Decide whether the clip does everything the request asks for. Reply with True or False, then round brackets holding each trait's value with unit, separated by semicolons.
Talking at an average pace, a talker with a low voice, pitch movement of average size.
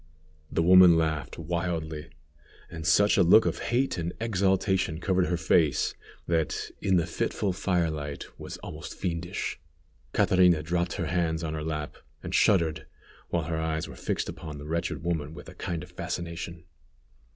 False (160 wpm; 85 Hz; 2.1 semitones)